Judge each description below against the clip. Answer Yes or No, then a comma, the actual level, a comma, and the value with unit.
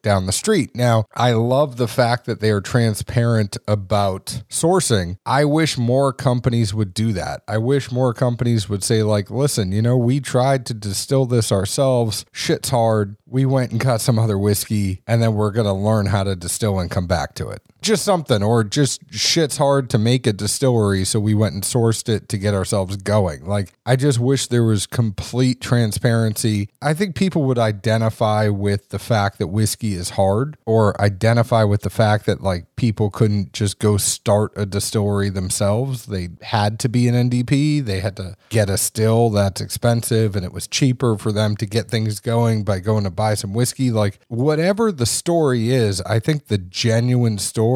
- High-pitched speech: No, low, 110 Hz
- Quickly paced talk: No, average, 195 wpm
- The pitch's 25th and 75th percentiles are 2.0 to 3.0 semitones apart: No, average, 3.4 semitones